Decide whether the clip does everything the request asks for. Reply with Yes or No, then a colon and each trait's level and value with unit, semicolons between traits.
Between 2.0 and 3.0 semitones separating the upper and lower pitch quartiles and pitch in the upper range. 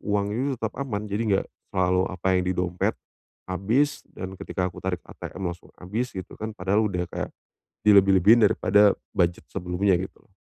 No: narrow, 2.5 semitones; very low, 95 Hz